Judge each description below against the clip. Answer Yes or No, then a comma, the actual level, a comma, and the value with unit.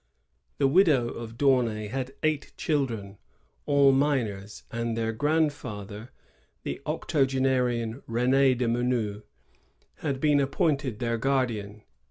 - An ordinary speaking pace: No, slow, 110 wpm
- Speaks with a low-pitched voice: Yes, low, 125 Hz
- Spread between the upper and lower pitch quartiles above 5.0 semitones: No, average, 3.5 semitones